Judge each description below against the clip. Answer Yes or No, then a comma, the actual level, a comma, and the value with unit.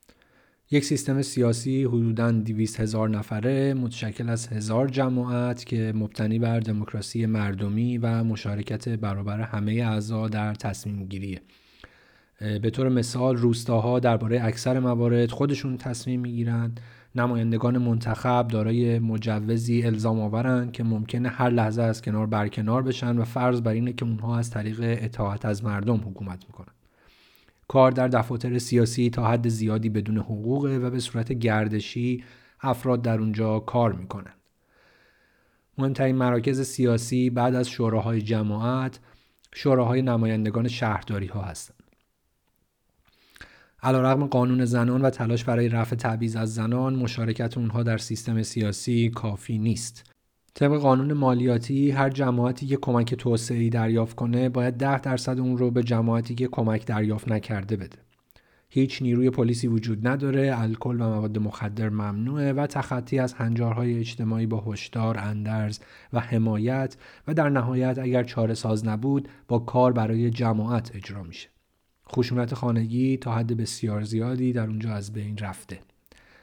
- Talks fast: No, average, 135 wpm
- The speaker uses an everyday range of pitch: No, narrow, 2.2 semitones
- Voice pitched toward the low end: Yes, low, 115 Hz